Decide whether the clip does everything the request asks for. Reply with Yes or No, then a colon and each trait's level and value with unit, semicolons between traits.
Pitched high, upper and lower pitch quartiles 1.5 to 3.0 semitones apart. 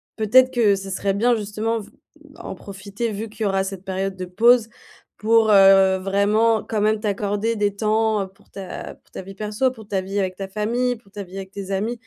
Yes: high, 205 Hz; narrow, 2.4 semitones